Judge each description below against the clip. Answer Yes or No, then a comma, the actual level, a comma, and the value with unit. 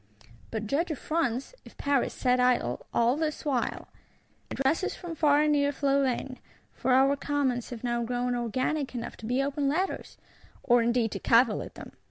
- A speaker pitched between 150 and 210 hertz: No, very high, 260 Hz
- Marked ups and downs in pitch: No, average, 3.0 semitones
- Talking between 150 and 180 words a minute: Yes, average, 175 wpm